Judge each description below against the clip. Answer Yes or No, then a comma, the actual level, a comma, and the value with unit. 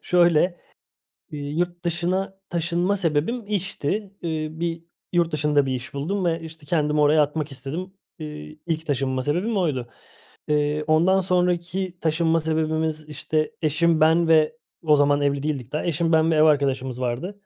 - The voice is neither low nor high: Yes, medium, 160 Hz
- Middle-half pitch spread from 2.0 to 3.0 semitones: Yes, average, 2.7 semitones